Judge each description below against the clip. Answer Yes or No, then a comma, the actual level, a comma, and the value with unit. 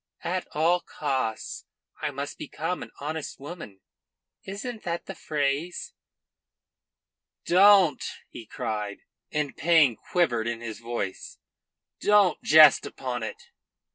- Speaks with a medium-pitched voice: Yes, medium, 150 Hz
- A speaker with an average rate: No, slow, 110 wpm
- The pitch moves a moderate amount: No, wide, 6.4 semitones